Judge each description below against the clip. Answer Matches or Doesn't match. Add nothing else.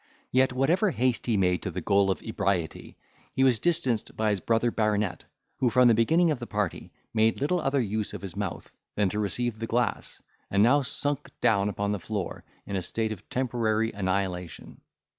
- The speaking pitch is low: Matches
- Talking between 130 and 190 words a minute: Doesn't match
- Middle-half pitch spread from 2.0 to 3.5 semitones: Doesn't match